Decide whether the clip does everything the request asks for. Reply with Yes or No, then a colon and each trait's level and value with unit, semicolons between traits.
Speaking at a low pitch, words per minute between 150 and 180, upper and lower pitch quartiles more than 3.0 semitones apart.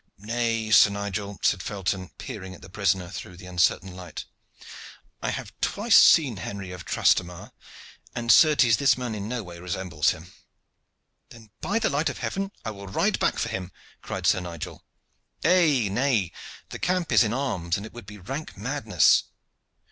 Yes: low, 100 Hz; average, 170 wpm; average, 5.0 semitones